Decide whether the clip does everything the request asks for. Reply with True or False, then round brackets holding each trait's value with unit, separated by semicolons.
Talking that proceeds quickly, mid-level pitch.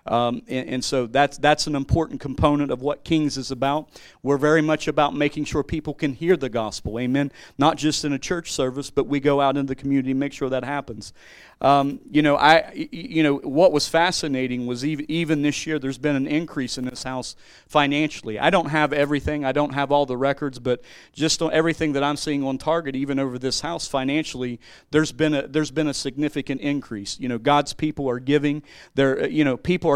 True (220 wpm; 145 Hz)